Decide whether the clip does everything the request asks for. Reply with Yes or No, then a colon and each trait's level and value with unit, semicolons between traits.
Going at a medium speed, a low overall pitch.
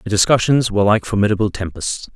Yes: average, 165 wpm; low, 105 Hz